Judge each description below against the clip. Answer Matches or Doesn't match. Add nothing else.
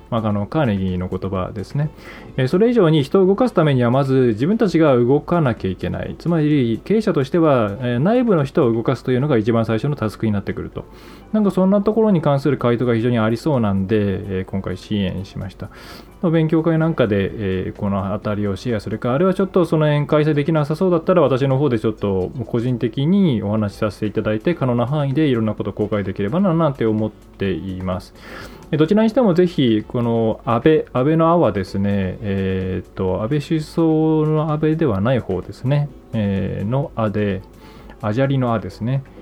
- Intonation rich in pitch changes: Matches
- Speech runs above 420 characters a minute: Doesn't match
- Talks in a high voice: Doesn't match